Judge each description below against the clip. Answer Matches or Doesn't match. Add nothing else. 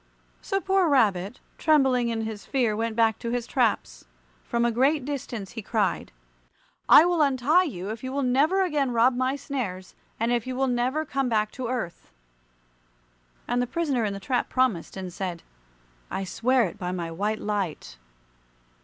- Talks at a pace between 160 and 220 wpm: Matches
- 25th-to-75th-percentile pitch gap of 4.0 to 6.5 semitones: Matches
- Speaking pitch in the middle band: Doesn't match